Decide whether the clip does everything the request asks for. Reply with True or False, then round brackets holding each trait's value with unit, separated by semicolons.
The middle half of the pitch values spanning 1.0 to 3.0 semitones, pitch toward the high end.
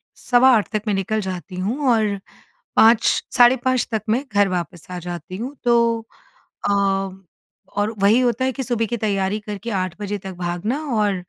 False (3.7 semitones; 210 Hz)